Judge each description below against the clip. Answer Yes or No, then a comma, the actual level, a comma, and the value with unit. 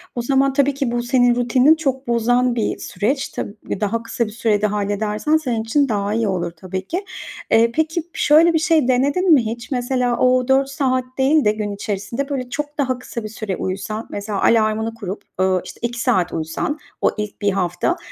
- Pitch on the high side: Yes, high, 235 Hz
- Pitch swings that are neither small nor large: Yes, average, 4.5 semitones